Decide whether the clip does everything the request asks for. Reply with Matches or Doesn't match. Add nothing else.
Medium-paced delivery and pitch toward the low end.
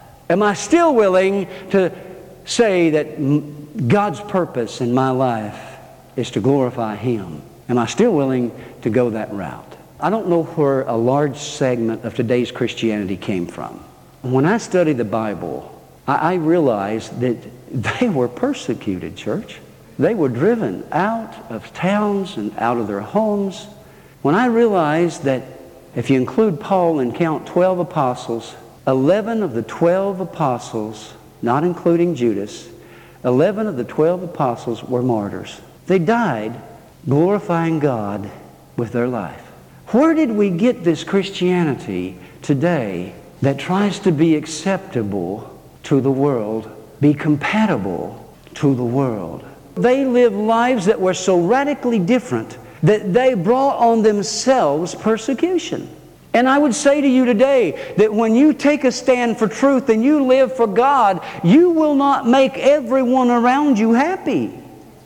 Doesn't match